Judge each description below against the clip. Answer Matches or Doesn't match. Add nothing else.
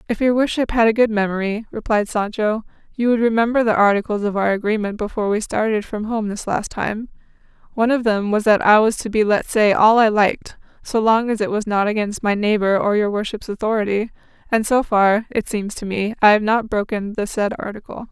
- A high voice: Matches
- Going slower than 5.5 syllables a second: Doesn't match